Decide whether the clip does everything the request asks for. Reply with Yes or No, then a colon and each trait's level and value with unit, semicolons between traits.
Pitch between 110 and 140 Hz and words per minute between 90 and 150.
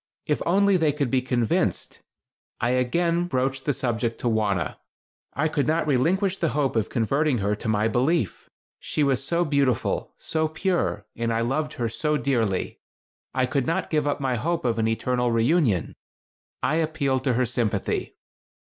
No: low, 135 Hz; average, 170 wpm